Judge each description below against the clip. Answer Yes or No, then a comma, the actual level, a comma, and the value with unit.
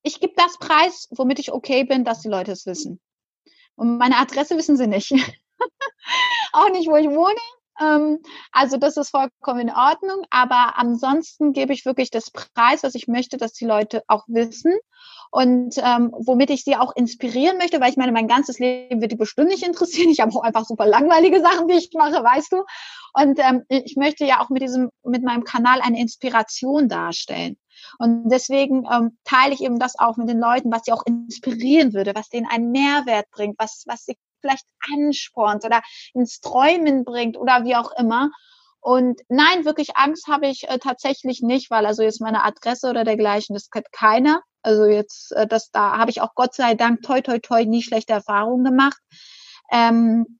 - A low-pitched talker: No, very high, 255 Hz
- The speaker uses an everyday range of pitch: Yes, average, 3.9 semitones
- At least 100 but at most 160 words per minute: No, fast, 190 wpm